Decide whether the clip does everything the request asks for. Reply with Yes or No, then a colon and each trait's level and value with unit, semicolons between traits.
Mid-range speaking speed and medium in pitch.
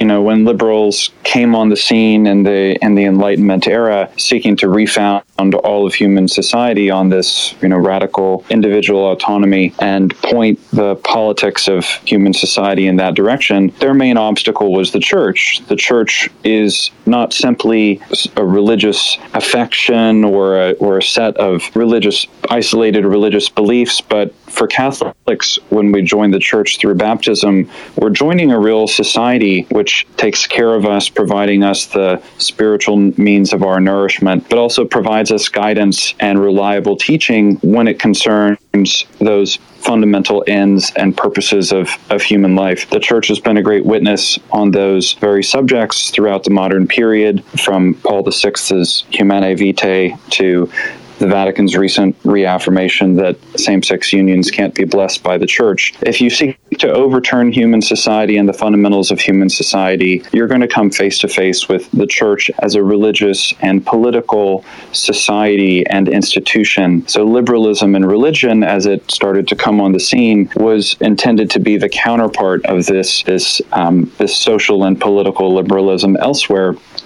No: average, 160 wpm; low, 100 Hz